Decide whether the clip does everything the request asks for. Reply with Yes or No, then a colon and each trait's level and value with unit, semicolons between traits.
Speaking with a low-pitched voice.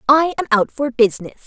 No: very high, 260 Hz